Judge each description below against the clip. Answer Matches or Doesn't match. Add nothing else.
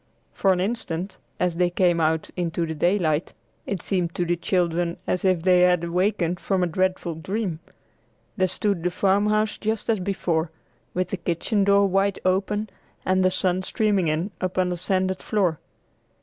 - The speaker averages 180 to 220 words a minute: Doesn't match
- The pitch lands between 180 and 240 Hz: Matches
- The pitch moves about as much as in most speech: Doesn't match